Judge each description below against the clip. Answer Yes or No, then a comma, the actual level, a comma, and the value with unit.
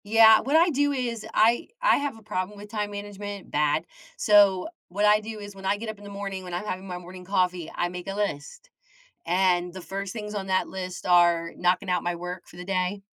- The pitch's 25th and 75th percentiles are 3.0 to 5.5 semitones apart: No, narrow, 2.6 semitones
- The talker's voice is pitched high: Yes, high, 195 Hz